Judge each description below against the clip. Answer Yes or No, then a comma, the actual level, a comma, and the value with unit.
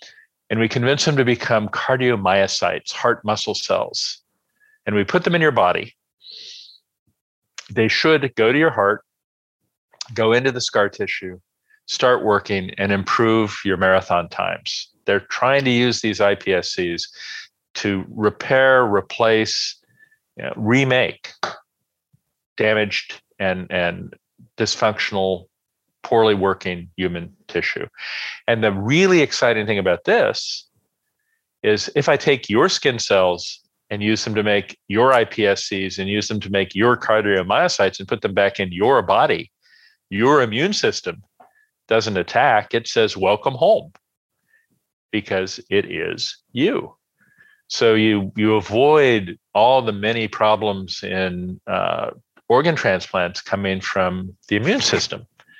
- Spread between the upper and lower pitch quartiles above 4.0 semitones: Yes, average, 4.6 semitones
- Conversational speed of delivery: No, slow, 130 wpm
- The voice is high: No, low, 110 Hz